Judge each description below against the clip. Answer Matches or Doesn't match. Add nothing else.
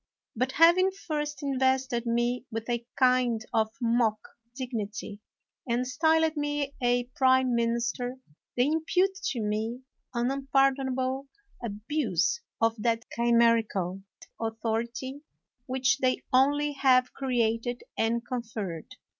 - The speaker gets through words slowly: Matches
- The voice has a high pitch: Matches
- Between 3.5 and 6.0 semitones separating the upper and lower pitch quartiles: Doesn't match